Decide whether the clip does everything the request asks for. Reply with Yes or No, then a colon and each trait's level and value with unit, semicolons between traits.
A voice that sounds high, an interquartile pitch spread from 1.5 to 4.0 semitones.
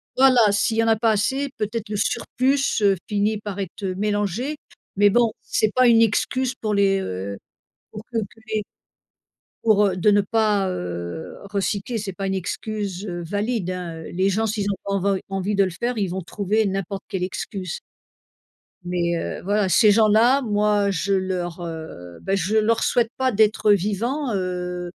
Yes: high, 205 Hz; average, 2.9 semitones